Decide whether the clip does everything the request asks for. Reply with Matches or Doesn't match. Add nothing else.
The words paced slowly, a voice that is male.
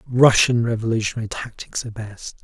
Matches